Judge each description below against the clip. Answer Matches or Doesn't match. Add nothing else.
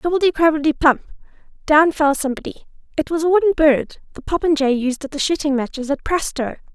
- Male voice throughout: Doesn't match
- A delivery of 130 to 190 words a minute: Matches